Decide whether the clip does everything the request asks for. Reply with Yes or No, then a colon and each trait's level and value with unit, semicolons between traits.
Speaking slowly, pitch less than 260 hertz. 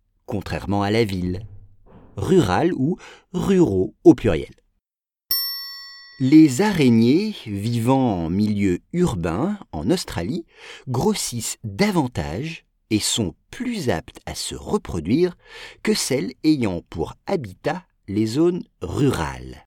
Yes: slow, 105 wpm; low, 135 Hz